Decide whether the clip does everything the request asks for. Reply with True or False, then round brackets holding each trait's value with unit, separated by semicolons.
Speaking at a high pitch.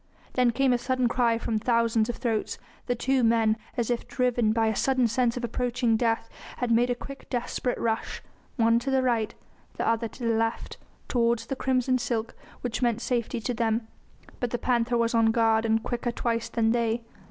True (235 Hz)